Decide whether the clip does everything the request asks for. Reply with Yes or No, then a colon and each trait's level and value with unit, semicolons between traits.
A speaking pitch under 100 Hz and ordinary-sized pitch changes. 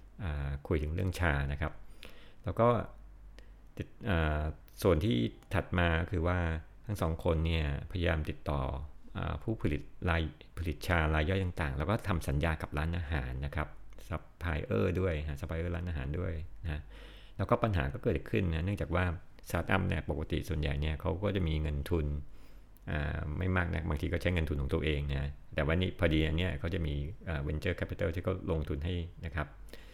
Yes: very low, 80 Hz; average, 3.3 semitones